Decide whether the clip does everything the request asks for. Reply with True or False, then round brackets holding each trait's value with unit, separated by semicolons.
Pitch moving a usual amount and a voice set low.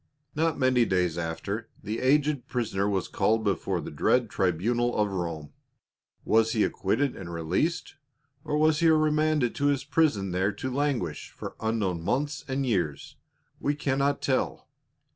False (6.8 semitones; 120 Hz)